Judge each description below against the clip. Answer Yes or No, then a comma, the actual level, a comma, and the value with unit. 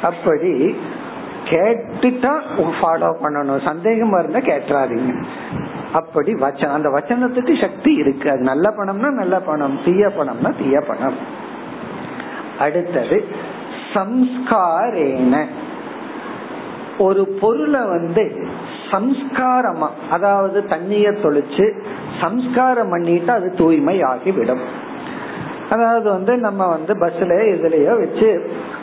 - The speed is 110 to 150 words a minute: No, average, 85 wpm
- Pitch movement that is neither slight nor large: No, wide, 6.3 semitones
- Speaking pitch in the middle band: No, high, 210 Hz